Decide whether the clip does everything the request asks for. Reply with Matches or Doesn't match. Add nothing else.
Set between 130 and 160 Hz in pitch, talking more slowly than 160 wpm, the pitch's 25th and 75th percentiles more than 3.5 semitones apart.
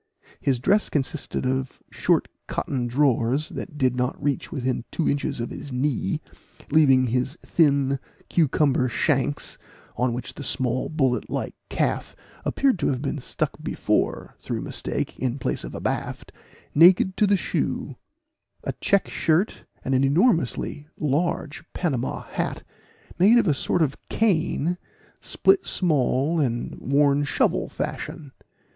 Matches